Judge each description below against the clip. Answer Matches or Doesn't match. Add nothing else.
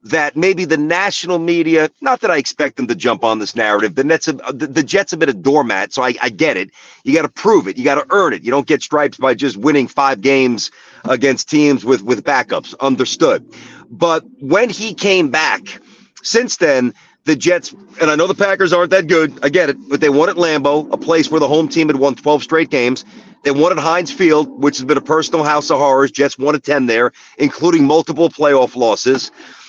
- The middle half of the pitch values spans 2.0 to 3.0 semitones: Doesn't match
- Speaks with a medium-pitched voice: Matches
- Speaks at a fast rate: Matches